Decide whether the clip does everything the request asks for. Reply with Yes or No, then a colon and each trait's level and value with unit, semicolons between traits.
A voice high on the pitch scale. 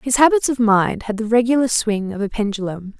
Yes: high, 225 Hz